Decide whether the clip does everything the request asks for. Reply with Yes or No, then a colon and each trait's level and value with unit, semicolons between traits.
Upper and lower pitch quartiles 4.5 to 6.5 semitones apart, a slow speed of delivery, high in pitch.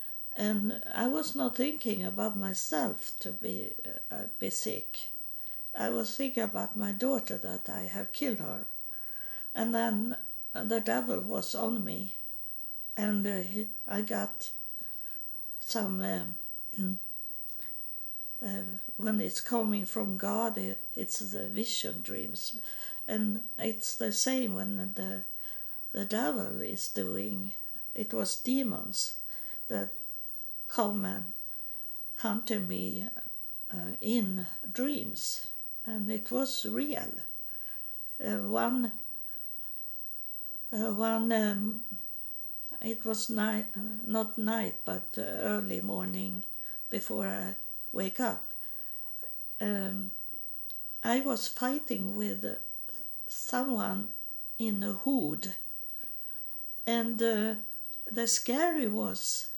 No: average, 2.7 semitones; slow, 105 wpm; high, 220 Hz